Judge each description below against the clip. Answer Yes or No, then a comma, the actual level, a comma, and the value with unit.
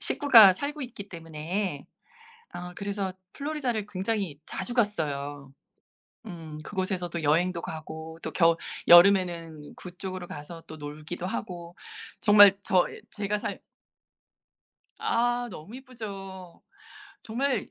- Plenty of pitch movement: No, average, 4.2 semitones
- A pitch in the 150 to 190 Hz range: Yes, medium, 185 Hz